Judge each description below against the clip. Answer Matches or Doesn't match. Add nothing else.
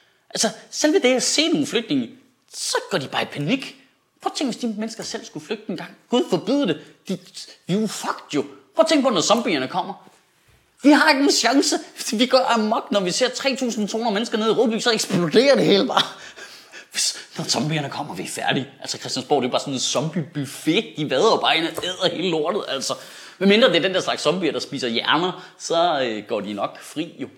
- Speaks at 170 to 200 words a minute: Doesn't match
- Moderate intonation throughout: Doesn't match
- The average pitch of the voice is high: Matches